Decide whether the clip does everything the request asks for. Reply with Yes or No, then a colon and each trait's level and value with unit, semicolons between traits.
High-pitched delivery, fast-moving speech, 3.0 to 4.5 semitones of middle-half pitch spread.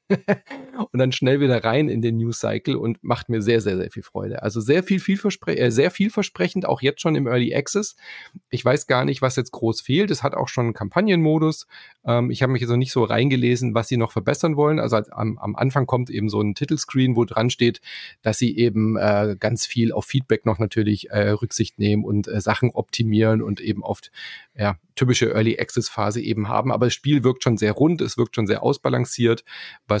No: low, 120 Hz; fast, 225 wpm; average, 4.0 semitones